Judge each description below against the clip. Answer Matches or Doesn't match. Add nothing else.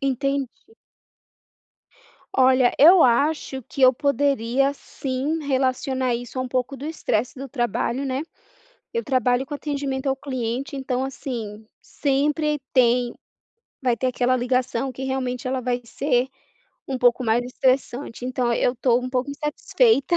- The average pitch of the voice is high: Matches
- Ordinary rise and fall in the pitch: Doesn't match